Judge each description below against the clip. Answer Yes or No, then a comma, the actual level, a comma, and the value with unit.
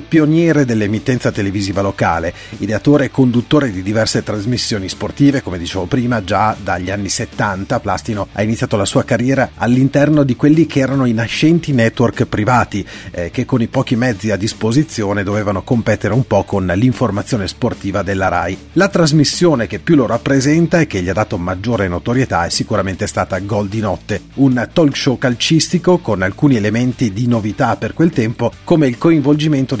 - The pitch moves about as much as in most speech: Yes, average, 4.8 semitones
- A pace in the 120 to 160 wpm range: No, fast, 170 wpm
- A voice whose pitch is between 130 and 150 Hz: No, low, 115 Hz